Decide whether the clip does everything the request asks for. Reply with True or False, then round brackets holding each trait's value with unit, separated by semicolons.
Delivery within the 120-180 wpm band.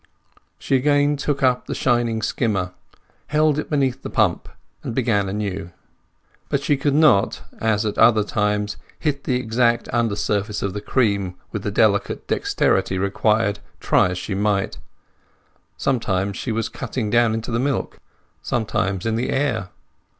True (155 wpm)